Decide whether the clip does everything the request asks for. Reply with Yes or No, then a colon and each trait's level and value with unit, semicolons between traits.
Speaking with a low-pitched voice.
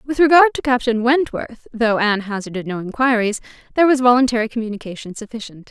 No: high, 235 Hz